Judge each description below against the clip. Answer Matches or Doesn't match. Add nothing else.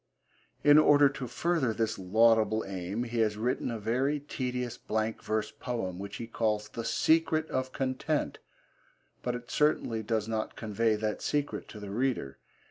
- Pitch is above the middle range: Doesn't match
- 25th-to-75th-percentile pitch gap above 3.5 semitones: Doesn't match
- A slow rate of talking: Doesn't match